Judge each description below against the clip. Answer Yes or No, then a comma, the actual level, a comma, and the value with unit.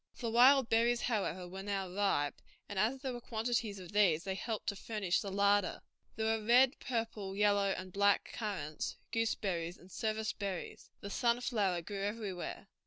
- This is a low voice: No, high, 205 Hz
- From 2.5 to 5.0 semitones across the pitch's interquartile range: Yes, average, 2.9 semitones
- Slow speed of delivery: No, average, 170 wpm